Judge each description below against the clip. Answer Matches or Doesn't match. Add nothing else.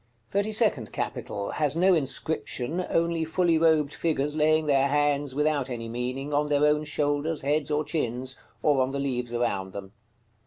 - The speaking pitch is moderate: Matches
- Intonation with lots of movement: Doesn't match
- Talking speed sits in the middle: Matches